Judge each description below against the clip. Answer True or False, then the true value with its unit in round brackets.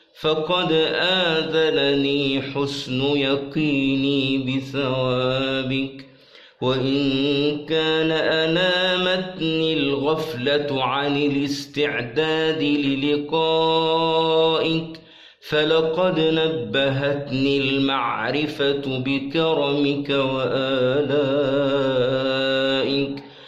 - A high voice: False (140 Hz)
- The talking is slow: True (45 wpm)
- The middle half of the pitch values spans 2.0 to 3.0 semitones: True (2.7 semitones)